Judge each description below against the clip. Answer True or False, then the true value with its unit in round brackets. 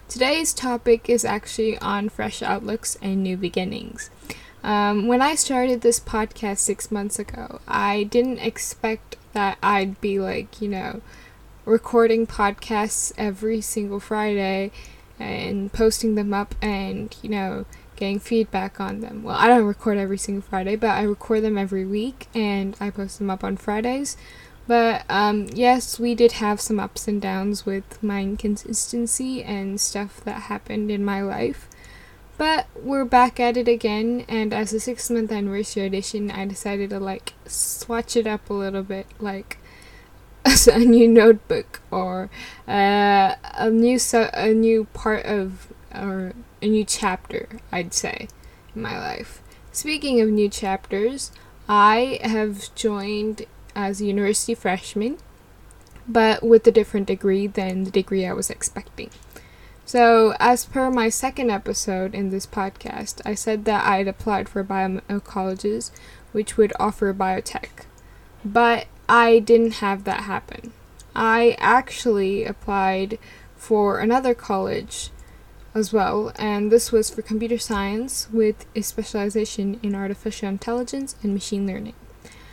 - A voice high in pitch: True (210 Hz)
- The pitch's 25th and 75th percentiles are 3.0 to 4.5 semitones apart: False (2.5 semitones)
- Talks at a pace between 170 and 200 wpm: False (145 wpm)